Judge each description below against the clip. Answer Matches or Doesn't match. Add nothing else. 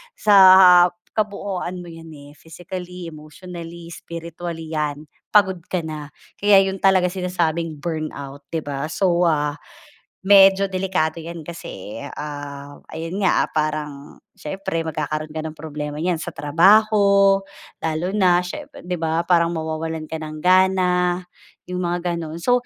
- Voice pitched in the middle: Matches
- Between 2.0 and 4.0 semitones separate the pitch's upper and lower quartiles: Matches